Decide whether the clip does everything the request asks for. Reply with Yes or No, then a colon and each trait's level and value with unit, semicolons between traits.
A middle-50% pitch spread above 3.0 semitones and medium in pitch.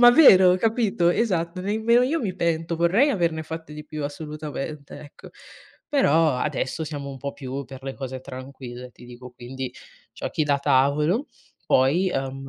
Yes: average, 5.2 semitones; medium, 150 Hz